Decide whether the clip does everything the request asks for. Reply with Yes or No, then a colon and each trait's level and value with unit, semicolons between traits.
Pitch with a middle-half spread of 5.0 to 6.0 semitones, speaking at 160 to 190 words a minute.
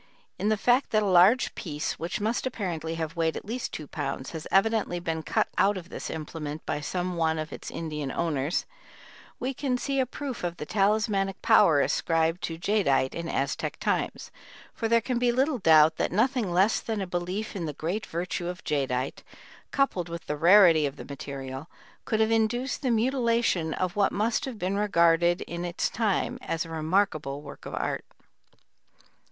Yes: wide, 5.4 semitones; average, 185 wpm